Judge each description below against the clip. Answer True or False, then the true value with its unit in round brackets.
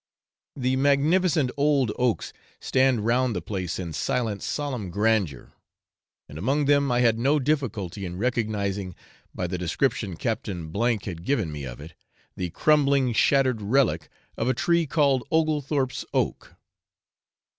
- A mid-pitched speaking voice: False (120 Hz)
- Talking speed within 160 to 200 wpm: False (140 wpm)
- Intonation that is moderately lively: False (6.4 semitones)